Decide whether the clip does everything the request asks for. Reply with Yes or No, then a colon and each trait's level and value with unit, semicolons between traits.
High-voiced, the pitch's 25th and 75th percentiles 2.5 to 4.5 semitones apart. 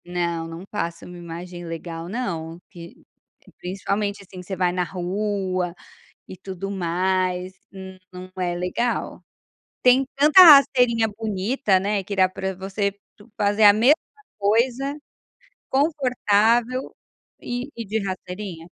Yes: high, 195 Hz; average, 3.8 semitones